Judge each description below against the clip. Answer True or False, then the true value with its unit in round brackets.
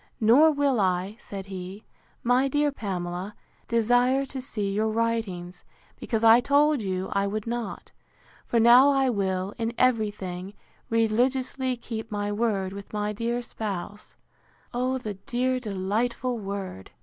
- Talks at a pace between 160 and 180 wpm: False (140 wpm)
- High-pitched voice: True (225 Hz)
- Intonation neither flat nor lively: True (3.8 semitones)